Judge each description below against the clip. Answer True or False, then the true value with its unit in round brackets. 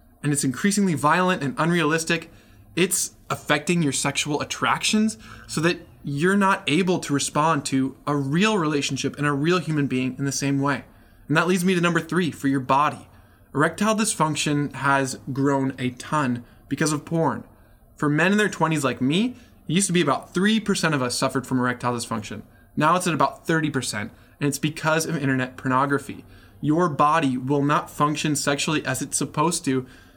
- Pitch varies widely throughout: False (3.8 semitones)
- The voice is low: False (145 Hz)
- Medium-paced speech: True (180 wpm)